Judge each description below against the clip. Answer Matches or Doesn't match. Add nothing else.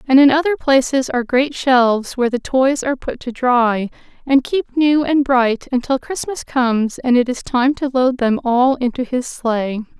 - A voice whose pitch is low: Doesn't match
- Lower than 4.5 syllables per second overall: Doesn't match